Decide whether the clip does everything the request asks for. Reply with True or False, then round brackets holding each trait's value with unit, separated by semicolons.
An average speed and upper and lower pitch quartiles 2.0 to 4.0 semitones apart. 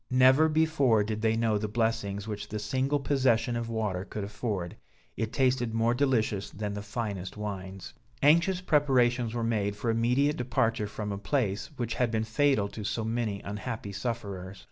True (170 wpm; 3.4 semitones)